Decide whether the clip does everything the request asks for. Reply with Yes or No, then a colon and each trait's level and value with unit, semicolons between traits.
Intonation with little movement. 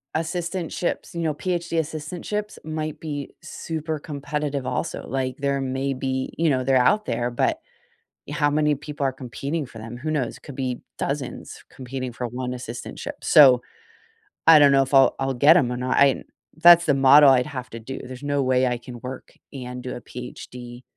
No: average, 3.2 semitones